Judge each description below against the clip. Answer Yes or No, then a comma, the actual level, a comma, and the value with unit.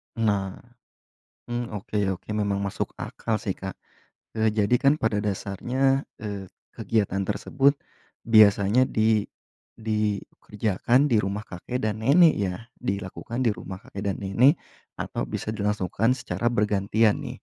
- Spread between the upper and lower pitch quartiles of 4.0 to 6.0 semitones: No, average, 2.8 semitones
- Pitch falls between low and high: No, low, 105 Hz